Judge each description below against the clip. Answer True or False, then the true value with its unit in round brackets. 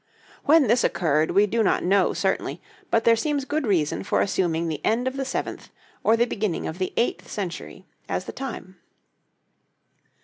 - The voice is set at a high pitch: True (215 Hz)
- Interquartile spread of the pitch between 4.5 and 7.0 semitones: True (5.6 semitones)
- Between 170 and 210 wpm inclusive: True (175 wpm)